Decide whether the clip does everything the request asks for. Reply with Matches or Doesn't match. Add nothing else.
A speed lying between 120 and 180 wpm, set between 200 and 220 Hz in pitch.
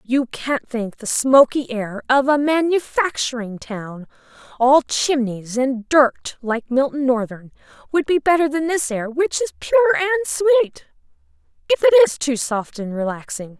Doesn't match